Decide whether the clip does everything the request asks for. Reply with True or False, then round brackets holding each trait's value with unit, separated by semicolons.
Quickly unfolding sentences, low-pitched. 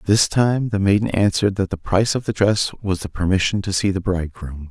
True (230 wpm; 95 Hz)